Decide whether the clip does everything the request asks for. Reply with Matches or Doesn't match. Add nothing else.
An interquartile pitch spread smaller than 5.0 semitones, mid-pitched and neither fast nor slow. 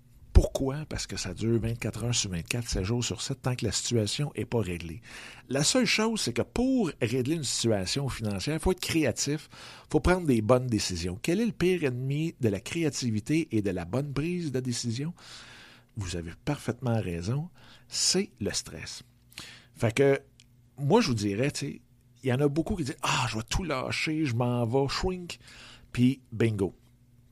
Doesn't match